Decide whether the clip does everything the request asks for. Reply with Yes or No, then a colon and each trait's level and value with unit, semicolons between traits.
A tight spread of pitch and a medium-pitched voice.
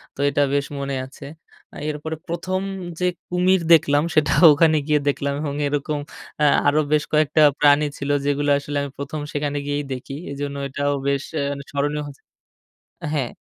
Yes: narrow, 1.3 semitones; medium, 145 Hz